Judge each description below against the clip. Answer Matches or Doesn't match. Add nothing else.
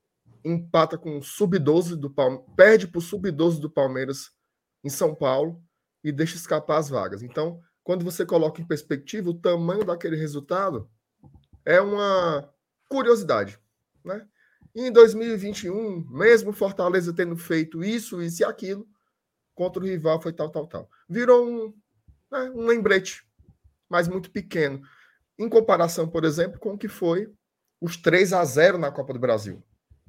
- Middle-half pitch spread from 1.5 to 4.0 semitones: Doesn't match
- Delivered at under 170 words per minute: Matches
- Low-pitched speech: Doesn't match